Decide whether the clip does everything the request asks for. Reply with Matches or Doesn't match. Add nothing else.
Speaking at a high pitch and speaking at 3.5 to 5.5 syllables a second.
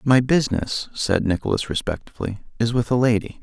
Doesn't match